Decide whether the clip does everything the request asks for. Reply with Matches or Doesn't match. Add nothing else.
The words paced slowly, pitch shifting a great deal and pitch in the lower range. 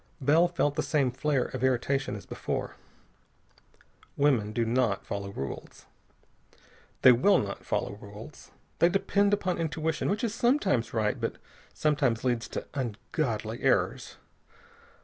Matches